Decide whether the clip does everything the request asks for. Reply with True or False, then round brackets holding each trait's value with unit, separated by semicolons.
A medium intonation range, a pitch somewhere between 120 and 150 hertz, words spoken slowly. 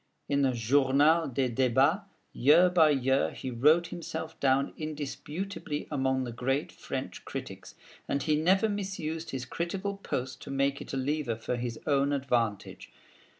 False (3.6 semitones; 140 Hz; 150 wpm)